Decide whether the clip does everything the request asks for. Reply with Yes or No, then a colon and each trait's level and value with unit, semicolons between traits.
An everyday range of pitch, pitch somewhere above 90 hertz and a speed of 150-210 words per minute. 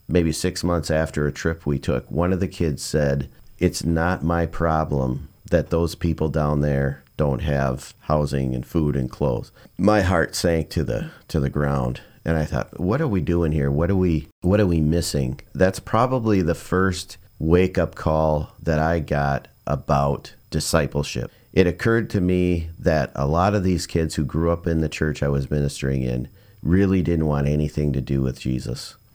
No: average, 3.8 semitones; very low, 80 Hz; average, 190 wpm